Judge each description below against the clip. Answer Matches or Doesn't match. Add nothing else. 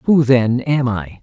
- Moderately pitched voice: Doesn't match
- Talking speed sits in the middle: Matches